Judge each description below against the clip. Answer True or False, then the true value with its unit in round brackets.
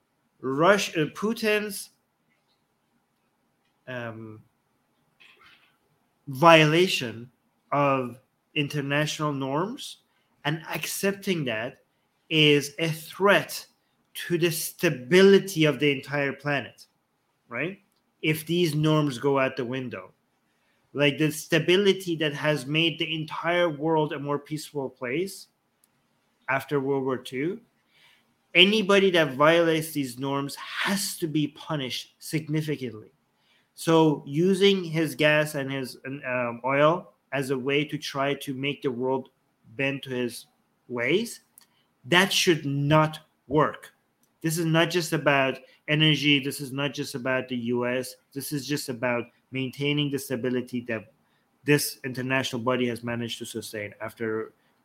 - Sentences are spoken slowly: True (120 wpm)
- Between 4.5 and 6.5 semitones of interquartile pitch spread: False (3.8 semitones)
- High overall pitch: False (145 Hz)